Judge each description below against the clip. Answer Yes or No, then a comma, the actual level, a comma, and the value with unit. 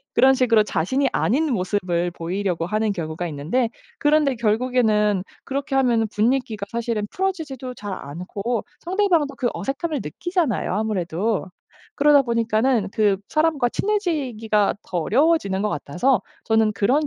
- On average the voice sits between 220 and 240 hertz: Yes, high, 230 Hz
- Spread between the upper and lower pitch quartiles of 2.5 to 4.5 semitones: No, average, 5.3 semitones